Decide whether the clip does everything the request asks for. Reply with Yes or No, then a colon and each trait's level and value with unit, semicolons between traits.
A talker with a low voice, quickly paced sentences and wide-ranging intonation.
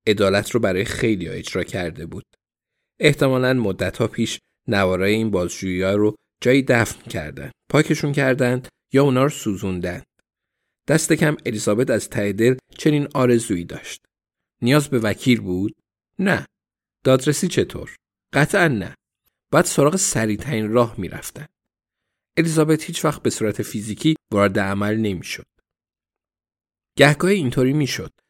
No: low, 120 Hz; average, 135 wpm; wide, 5.8 semitones